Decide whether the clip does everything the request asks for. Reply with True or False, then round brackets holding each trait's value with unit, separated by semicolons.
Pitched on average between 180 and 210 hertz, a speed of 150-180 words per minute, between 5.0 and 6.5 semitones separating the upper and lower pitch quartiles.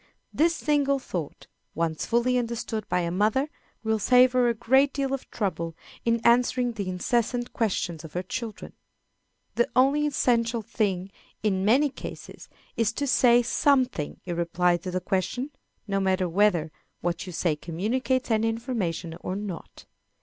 False (220 Hz; 155 wpm; 5.6 semitones)